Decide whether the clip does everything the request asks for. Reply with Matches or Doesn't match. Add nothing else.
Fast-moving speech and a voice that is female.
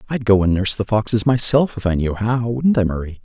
Doesn't match